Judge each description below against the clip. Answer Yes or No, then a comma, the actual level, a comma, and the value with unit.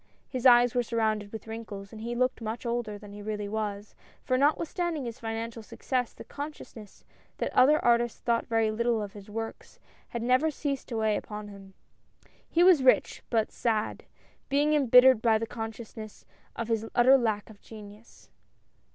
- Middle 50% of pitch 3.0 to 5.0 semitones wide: No, narrow, 2.6 semitones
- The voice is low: No, high, 230 Hz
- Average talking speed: Yes, average, 170 wpm